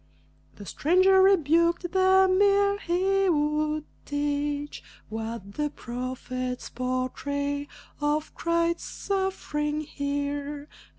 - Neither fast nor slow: No, slow, 85 wpm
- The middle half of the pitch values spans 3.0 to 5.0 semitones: Yes, average, 4.3 semitones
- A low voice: No, very high, 295 Hz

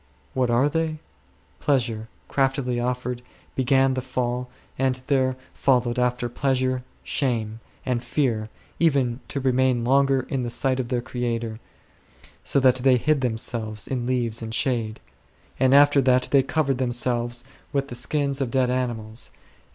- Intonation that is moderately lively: No, narrow, 1.9 semitones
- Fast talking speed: No, average, 155 wpm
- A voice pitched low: Yes, low, 125 Hz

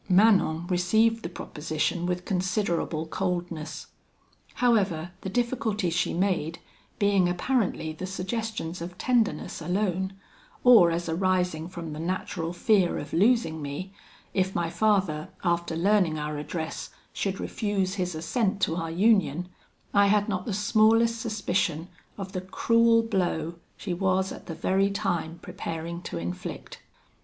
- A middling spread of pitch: Yes, average, 3.7 semitones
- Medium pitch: Yes, medium, 180 Hz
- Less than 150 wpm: Yes, slow, 135 wpm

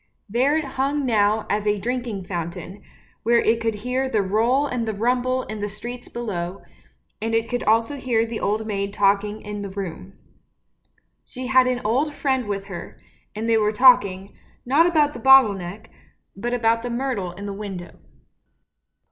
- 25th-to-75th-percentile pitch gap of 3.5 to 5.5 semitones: Yes, average, 3.8 semitones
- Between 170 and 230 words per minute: Yes, average, 175 wpm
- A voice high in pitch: Yes, high, 225 Hz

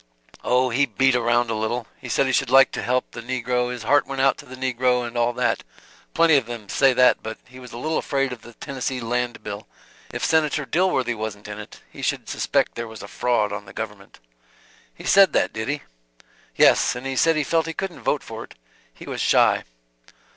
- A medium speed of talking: No, fast, 225 wpm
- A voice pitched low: Yes, low, 125 Hz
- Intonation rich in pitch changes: No, narrow, 2.6 semitones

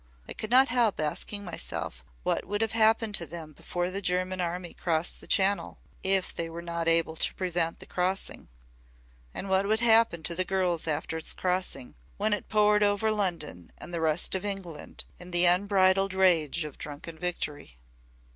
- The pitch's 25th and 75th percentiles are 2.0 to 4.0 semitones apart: Yes, average, 3.3 semitones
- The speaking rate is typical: Yes, average, 180 wpm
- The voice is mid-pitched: Yes, medium, 180 Hz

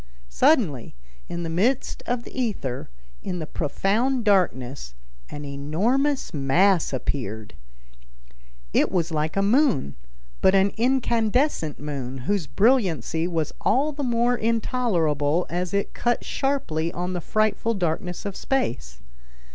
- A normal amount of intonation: No, wide, 7.9 semitones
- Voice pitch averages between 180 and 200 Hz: Yes, medium, 185 Hz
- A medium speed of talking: No, slow, 125 wpm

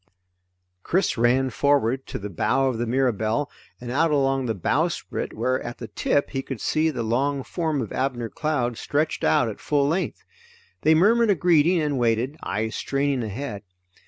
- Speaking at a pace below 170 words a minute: No, average, 175 wpm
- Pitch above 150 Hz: No, low, 135 Hz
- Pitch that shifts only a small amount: No, average, 3.8 semitones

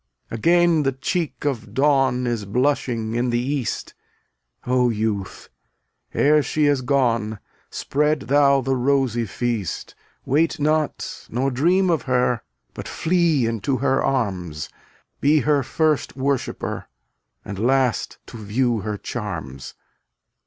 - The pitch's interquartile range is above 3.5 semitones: Yes, average, 4.0 semitones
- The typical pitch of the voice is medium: No, low, 130 Hz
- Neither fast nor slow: No, slow, 125 wpm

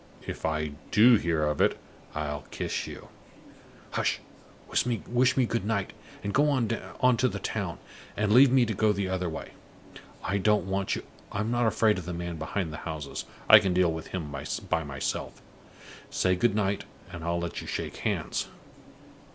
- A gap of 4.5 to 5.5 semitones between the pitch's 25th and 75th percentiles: Yes, average, 5.2 semitones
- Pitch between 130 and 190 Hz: No, very low, 95 Hz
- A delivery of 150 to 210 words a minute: Yes, average, 175 wpm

